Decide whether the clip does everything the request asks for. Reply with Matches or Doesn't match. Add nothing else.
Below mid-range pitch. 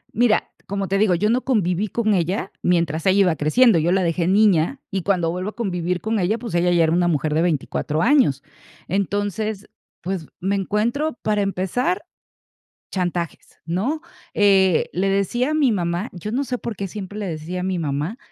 Doesn't match